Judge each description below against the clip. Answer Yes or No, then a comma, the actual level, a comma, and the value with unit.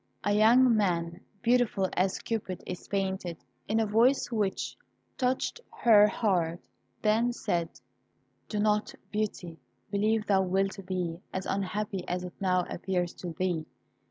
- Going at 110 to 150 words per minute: Yes, slow, 135 wpm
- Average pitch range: Yes, average, 3.1 semitones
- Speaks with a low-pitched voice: No, high, 195 Hz